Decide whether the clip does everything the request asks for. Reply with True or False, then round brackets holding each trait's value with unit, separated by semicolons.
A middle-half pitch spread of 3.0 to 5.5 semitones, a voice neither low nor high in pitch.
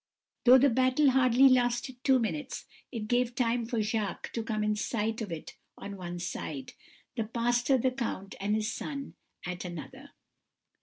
False (3.4 semitones; 230 Hz)